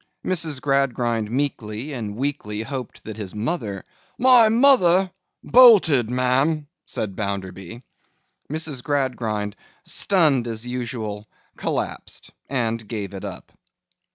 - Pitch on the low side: Yes, low, 125 Hz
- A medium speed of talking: No, slow, 105 wpm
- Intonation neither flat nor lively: No, wide, 5.8 semitones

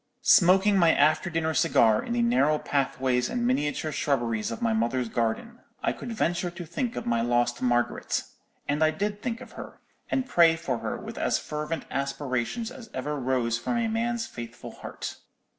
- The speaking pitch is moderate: Yes, medium, 155 Hz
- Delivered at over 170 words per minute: Yes, average, 180 wpm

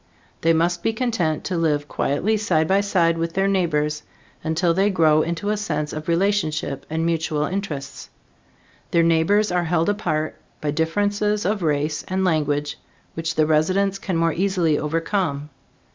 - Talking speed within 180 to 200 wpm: No, average, 160 wpm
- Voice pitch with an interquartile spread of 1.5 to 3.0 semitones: No, average, 3.9 semitones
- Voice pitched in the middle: Yes, medium, 165 Hz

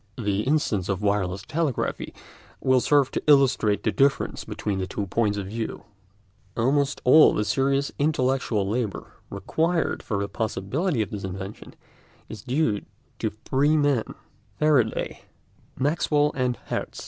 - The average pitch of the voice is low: Yes, low, 120 Hz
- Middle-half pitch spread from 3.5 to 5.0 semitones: No, wide, 5.6 semitones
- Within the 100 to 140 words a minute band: Yes, slow, 135 wpm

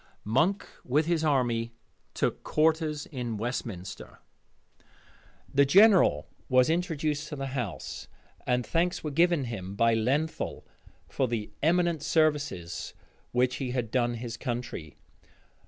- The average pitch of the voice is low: Yes, low, 130 Hz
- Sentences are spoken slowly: Yes, slow, 125 wpm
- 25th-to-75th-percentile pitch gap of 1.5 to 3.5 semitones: No, average, 5.0 semitones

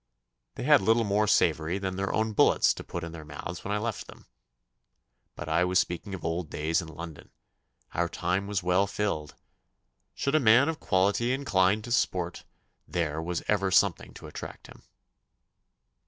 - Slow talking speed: No, average, 175 wpm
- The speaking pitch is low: Yes, very low, 95 Hz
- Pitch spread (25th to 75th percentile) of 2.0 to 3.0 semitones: No, average, 3.8 semitones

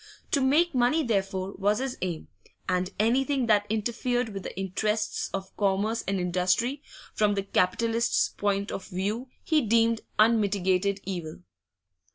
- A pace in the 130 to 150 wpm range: Yes, average, 140 wpm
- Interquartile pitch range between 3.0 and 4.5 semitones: Yes, average, 3.5 semitones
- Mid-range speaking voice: No, high, 210 Hz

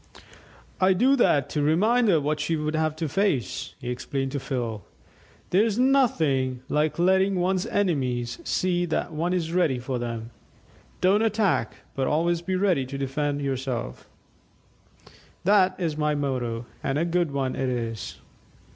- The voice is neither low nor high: Yes, medium, 155 Hz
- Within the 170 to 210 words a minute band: No, average, 155 wpm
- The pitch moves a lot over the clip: Yes, wide, 5.7 semitones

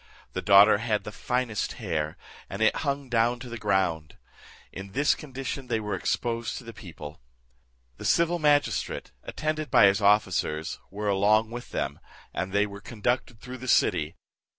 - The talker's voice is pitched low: Yes, low, 110 Hz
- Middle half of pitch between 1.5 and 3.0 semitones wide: No, average, 4.1 semitones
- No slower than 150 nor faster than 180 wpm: Yes, average, 165 wpm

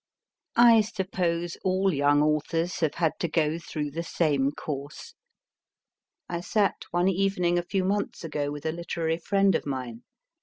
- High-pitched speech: No, medium, 170 Hz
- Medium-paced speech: Yes, average, 155 wpm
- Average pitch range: Yes, average, 3.8 semitones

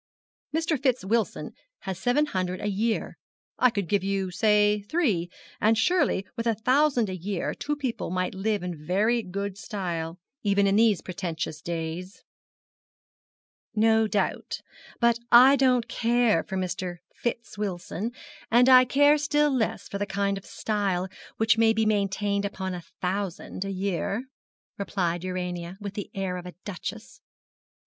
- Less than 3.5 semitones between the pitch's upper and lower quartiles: No, average, 3.8 semitones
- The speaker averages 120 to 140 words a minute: No, average, 155 wpm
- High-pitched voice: Yes, high, 200 Hz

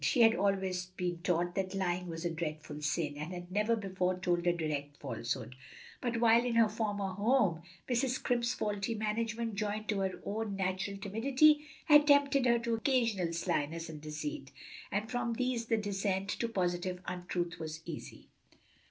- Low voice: No, high, 195 Hz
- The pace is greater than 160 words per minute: Yes, average, 170 wpm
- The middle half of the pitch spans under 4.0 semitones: No, average, 4.7 semitones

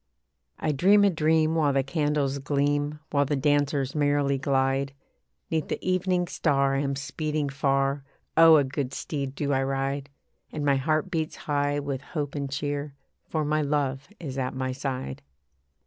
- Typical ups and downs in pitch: No, narrow, 1.8 semitones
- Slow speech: No, average, 165 wpm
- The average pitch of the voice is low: No, medium, 145 Hz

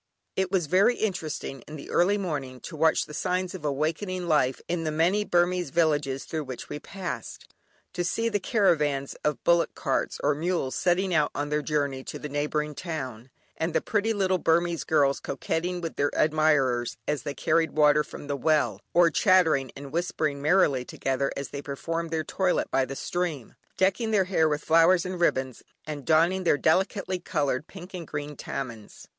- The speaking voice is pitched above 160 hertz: No, medium, 155 Hz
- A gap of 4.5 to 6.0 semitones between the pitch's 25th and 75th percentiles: No, average, 3.8 semitones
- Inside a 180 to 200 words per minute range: Yes, average, 185 wpm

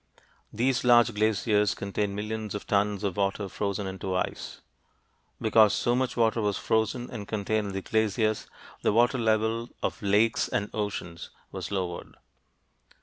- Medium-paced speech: Yes, average, 145 wpm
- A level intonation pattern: Yes, narrow, 2.0 semitones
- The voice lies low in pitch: Yes, low, 105 Hz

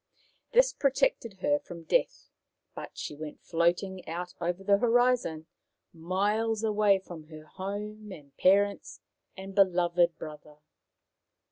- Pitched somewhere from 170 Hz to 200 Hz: Yes, high, 190 Hz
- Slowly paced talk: Yes, slow, 120 wpm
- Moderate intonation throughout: Yes, average, 3.9 semitones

